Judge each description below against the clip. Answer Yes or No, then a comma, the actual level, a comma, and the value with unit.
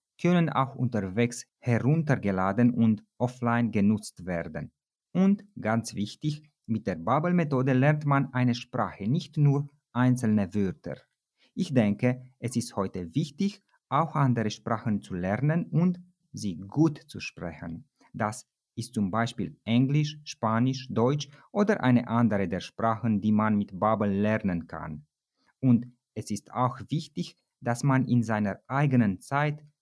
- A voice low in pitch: Yes, low, 120 Hz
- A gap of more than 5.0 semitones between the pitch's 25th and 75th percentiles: Yes, wide, 5.4 semitones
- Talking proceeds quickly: No, average, 135 wpm